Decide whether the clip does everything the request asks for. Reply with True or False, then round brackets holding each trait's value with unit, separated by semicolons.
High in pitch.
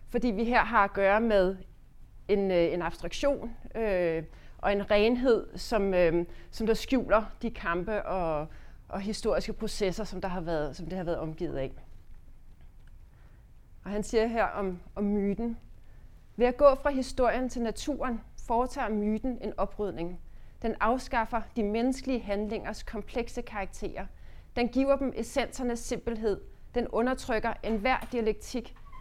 True (220 Hz)